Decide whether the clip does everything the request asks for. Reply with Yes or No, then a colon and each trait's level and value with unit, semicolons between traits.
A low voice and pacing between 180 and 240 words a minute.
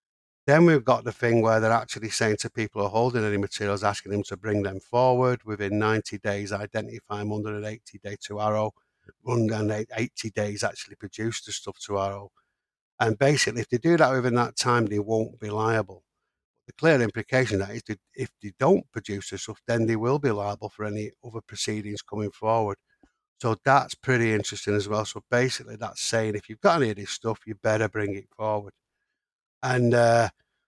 Yes: low, 110 Hz; fast, 205 wpm